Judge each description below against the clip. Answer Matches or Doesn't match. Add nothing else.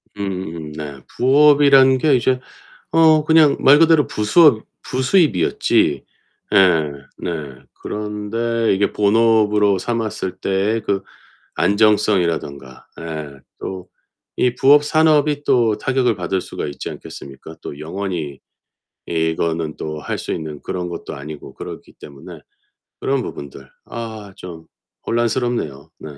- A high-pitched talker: Doesn't match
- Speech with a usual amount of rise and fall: Doesn't match